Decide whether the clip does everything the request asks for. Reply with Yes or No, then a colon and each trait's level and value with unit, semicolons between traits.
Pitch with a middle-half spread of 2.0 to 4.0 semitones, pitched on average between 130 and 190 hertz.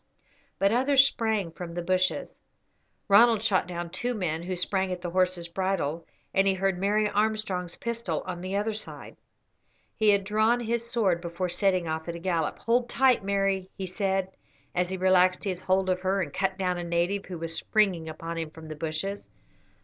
Yes: average, 2.8 semitones; medium, 185 Hz